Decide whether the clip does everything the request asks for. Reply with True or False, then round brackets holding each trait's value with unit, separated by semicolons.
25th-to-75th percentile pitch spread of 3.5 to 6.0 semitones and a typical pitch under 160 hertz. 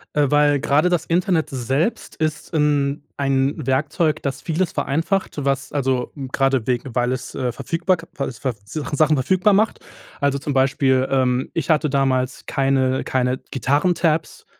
False (3.0 semitones; 140 Hz)